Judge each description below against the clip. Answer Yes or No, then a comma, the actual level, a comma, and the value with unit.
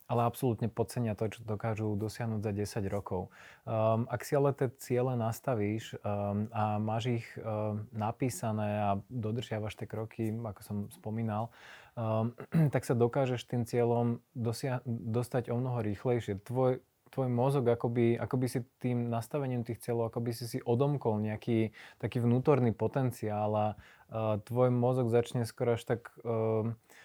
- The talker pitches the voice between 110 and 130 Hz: Yes, low, 115 Hz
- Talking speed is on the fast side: No, average, 150 wpm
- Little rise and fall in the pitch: Yes, narrow, 2.3 semitones